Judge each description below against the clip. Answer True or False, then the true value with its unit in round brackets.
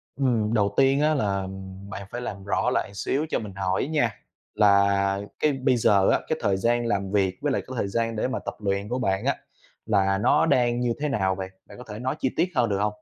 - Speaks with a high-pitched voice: False (105 Hz)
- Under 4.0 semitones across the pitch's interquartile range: False (4.3 semitones)